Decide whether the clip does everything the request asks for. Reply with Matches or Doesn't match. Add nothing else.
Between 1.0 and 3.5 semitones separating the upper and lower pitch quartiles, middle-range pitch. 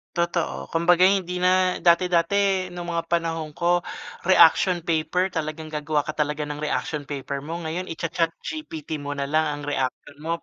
Matches